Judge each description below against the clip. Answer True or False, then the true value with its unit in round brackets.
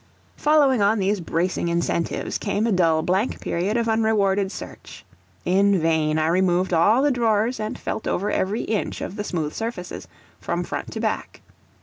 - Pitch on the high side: True (200 Hz)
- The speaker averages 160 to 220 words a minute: True (165 wpm)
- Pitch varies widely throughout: False (4.0 semitones)